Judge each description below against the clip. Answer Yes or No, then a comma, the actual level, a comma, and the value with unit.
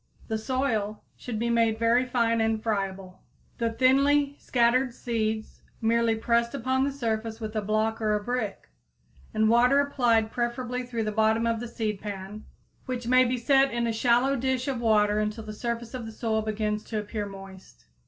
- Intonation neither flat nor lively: No, narrow, 2.3 semitones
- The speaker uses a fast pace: No, average, 180 wpm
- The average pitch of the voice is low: No, high, 230 Hz